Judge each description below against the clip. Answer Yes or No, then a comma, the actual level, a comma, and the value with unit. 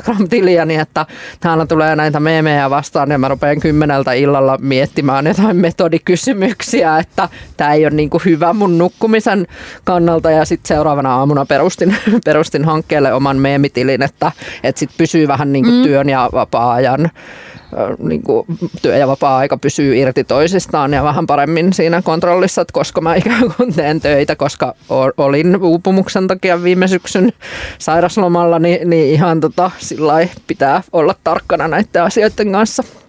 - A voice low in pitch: No, medium, 165 Hz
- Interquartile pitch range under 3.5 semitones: No, average, 3.8 semitones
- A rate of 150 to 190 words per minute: No, average, 140 wpm